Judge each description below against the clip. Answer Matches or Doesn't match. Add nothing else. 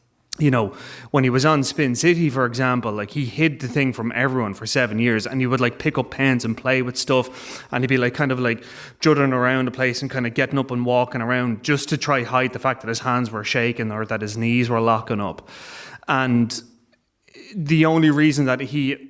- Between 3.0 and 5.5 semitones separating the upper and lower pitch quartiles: Doesn't match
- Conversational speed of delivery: Doesn't match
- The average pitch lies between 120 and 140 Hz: Matches